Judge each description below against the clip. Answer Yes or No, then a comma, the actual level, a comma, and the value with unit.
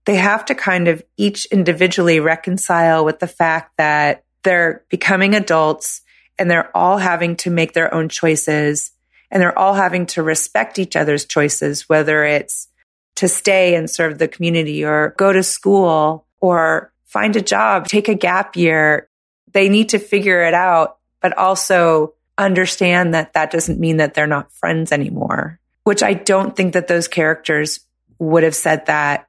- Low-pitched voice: No, medium, 170 Hz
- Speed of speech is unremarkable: Yes, average, 170 wpm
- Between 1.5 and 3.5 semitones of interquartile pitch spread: Yes, average, 3.1 semitones